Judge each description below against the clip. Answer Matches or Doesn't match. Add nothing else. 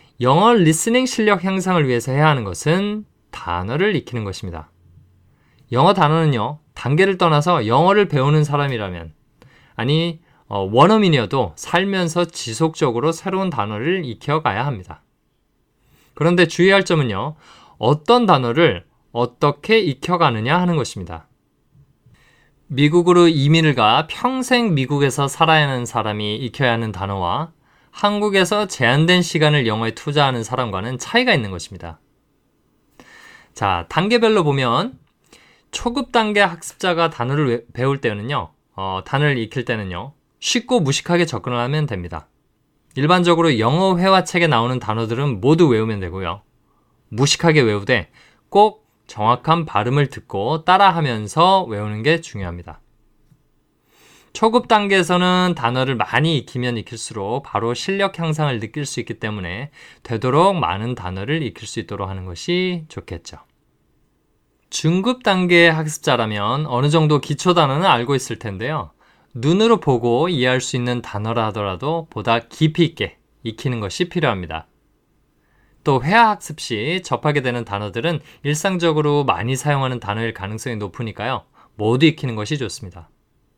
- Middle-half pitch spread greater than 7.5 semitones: Doesn't match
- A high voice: Doesn't match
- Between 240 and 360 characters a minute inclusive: Matches